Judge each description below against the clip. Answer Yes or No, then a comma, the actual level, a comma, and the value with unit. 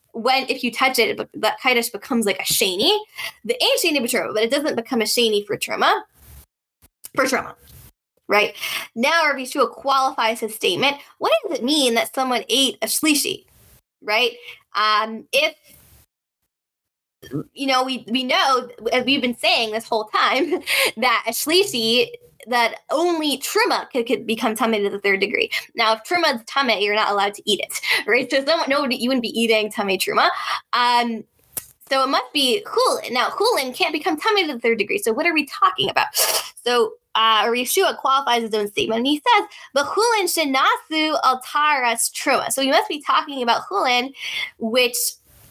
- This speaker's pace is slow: No, average, 180 wpm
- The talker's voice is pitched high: Yes, very high, 260 Hz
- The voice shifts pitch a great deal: Yes, wide, 5.9 semitones